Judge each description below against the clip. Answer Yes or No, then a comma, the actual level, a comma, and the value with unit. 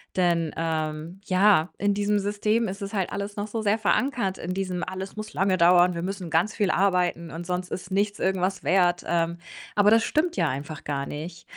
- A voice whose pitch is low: No, medium, 185 Hz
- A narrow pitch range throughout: No, average, 3.0 semitones